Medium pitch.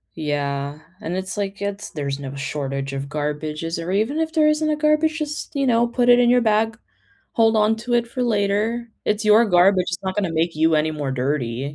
No: high, 200 Hz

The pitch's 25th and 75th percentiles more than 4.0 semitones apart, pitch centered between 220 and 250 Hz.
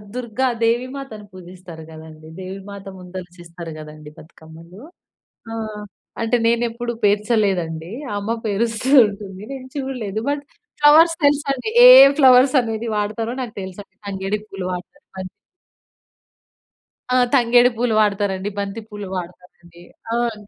No: average, 4.6 semitones; high, 205 Hz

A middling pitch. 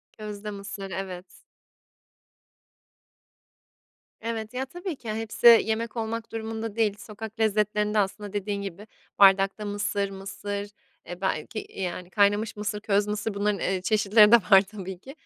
No: high, 210 Hz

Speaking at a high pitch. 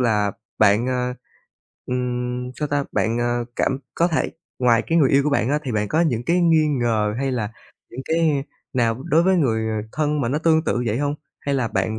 No: low, 125 Hz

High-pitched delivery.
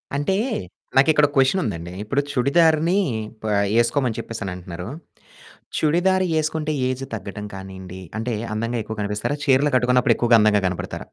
No: low, 125 Hz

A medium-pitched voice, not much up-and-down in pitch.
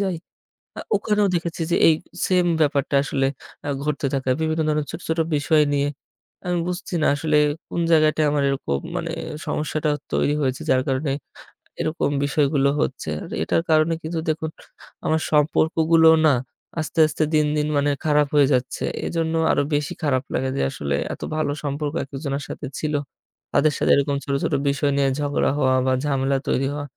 Yes: medium, 150 Hz; narrow, 2.2 semitones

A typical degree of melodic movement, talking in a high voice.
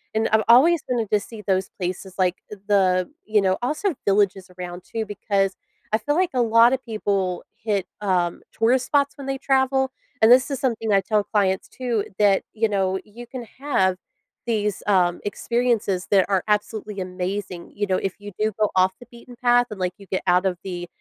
Yes: average, 4.0 semitones; high, 210 Hz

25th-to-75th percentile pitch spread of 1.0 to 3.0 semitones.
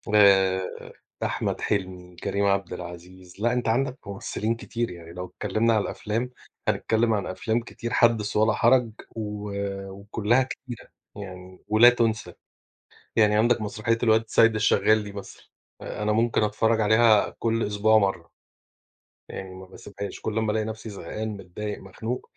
Yes: narrow, 2.5 semitones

